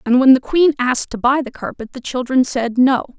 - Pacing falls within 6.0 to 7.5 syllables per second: No, 5.5 syllables/s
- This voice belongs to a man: No, female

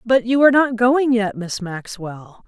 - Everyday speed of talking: Yes, average, 195 wpm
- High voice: Yes, high, 225 Hz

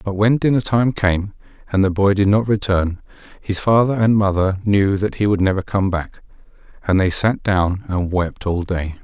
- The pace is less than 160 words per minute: No, average, 200 wpm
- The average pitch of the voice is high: No, low, 100 Hz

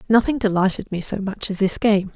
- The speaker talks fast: Yes, fast, 220 wpm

